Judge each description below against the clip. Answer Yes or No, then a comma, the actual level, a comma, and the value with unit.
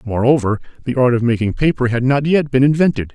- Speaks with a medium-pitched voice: No, low, 130 Hz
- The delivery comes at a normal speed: No, fast, 210 wpm